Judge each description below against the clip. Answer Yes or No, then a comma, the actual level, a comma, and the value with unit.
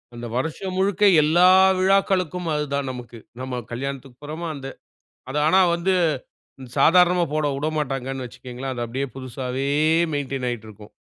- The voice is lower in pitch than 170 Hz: Yes, medium, 140 Hz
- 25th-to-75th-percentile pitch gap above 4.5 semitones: Yes, average, 4.9 semitones